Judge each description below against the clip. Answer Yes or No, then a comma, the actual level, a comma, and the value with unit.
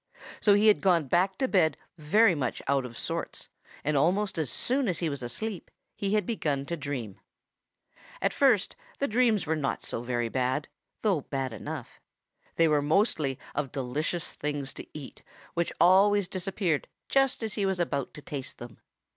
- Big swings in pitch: Yes, wide, 6.4 semitones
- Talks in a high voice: No, medium, 160 Hz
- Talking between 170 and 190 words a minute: Yes, average, 175 wpm